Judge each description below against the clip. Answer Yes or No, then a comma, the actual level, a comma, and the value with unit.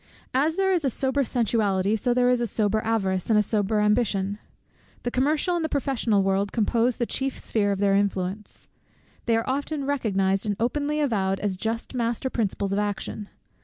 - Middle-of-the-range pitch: No, high, 225 Hz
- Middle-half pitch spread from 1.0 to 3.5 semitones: No, average, 4.4 semitones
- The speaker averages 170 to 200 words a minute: Yes, average, 190 wpm